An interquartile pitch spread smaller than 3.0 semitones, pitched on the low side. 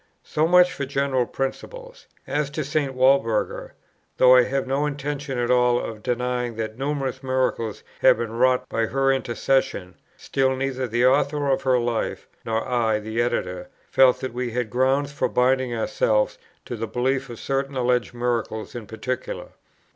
Yes: narrow, 2.4 semitones; low, 130 Hz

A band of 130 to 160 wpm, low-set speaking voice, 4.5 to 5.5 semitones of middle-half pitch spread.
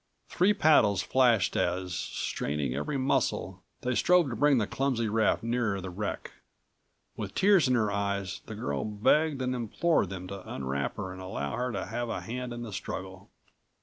No: average, 180 wpm; low, 110 Hz; average, 5.2 semitones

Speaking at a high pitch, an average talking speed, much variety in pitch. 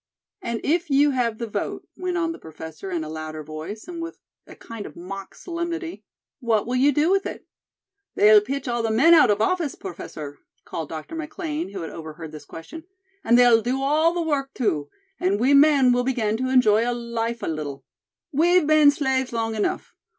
Yes: high, 245 Hz; average, 195 wpm; wide, 7.3 semitones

